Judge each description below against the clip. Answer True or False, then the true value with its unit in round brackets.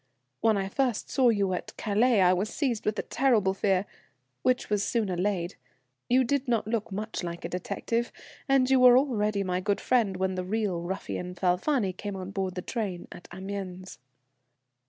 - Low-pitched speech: False (200 Hz)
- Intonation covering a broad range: False (4.1 semitones)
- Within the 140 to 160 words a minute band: False (180 wpm)